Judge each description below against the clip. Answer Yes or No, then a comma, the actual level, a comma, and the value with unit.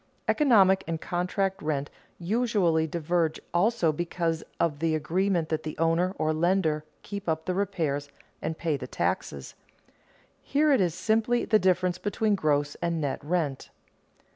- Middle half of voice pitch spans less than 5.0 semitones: Yes, average, 3.5 semitones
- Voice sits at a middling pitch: Yes, medium, 170 Hz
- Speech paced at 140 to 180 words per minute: Yes, average, 145 wpm